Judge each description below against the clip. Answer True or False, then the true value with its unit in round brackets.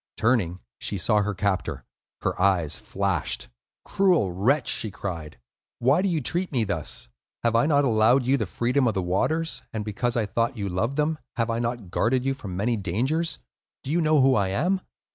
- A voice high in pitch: False (115 Hz)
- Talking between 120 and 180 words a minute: False (200 wpm)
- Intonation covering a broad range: True (5.8 semitones)